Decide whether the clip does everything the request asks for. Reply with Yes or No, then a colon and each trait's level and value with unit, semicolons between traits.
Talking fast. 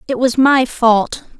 No: average, 170 wpm